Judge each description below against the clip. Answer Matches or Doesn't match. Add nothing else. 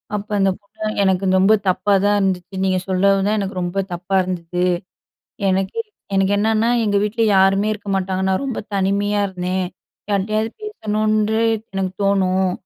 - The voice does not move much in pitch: Matches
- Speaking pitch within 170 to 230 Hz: Matches